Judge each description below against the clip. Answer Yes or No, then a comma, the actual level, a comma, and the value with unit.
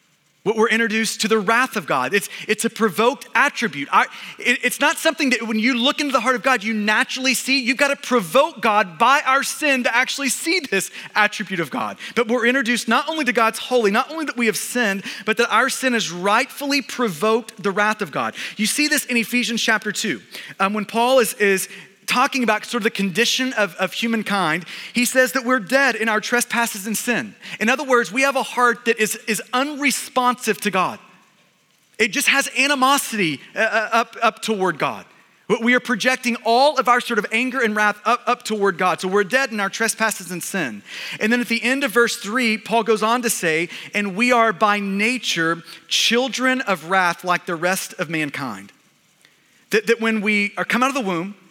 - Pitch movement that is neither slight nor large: Yes, average, 3.6 semitones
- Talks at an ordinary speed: No, fast, 210 wpm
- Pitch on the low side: No, high, 225 Hz